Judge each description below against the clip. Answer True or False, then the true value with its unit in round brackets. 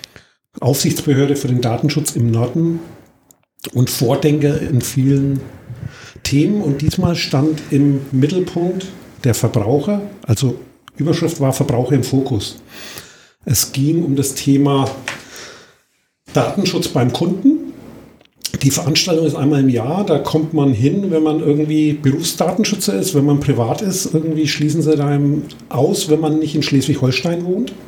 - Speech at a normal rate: True (135 wpm)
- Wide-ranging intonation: False (3.2 semitones)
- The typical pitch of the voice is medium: True (145 Hz)